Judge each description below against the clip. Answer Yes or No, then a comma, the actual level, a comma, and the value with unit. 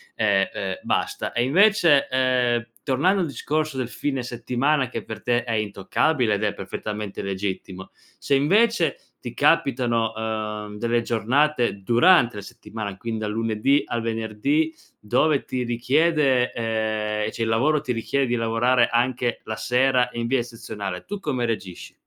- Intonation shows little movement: No, average, 3.8 semitones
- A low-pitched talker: Yes, low, 120 Hz